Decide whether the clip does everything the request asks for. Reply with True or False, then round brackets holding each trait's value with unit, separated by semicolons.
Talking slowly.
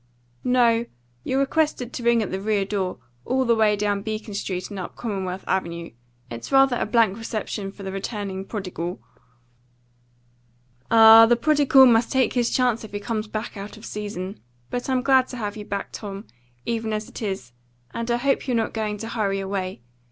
False (190 wpm)